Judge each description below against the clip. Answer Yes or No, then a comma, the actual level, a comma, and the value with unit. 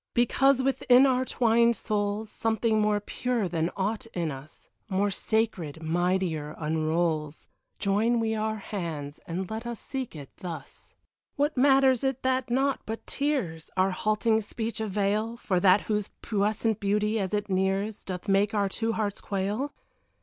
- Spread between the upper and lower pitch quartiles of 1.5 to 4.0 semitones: Yes, average, 3.7 semitones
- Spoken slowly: No, average, 150 wpm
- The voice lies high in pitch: Yes, high, 210 Hz